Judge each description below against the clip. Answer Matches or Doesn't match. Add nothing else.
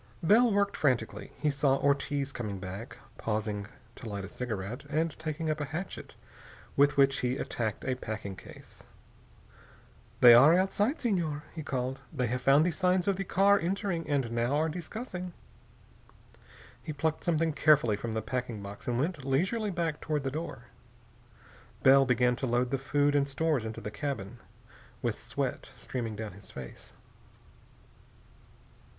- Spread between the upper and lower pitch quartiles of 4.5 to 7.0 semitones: Matches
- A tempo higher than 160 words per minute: Doesn't match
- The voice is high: Doesn't match